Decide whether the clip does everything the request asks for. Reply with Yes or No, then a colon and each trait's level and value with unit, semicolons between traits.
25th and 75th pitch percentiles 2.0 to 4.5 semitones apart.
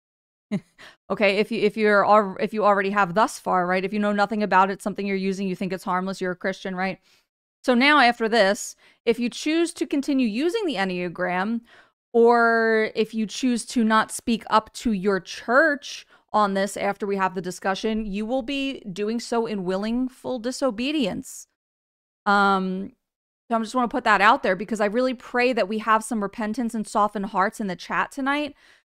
Yes: average, 3.6 semitones